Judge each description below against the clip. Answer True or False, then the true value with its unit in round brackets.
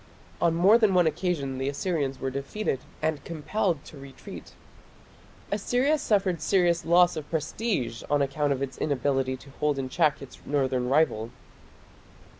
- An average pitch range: True (4.6 semitones)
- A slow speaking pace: False (150 wpm)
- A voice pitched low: False (150 Hz)